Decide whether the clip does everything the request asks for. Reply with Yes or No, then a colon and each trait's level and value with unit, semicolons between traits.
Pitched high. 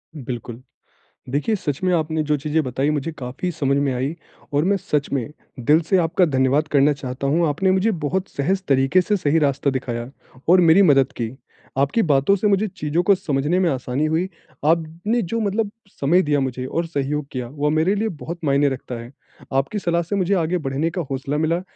No: medium, 150 Hz